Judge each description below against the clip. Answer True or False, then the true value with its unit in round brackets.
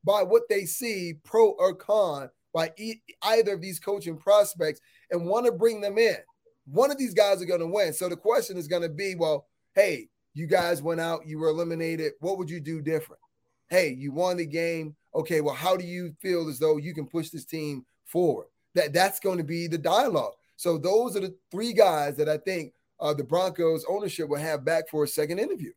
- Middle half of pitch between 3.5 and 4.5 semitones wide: True (4.2 semitones)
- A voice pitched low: False (175 Hz)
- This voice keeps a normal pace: False (220 wpm)